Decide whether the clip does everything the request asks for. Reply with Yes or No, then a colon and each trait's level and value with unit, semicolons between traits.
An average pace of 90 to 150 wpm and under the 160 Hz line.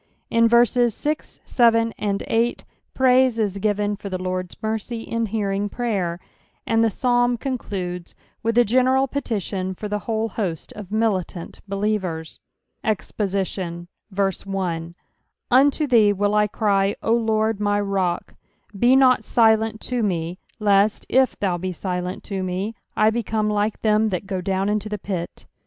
No: average, 145 wpm; high, 210 Hz